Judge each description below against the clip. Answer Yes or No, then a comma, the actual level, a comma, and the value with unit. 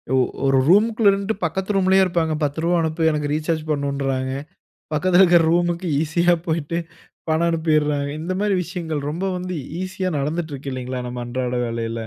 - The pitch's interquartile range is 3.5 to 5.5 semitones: Yes, average, 4.0 semitones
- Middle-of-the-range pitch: Yes, medium, 160 Hz